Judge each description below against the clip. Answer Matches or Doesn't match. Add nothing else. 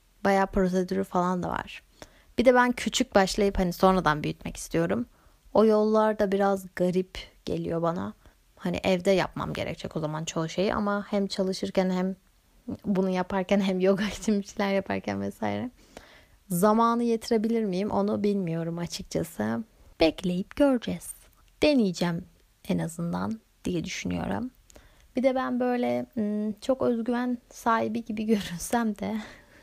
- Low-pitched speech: Doesn't match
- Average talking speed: Matches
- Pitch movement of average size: Matches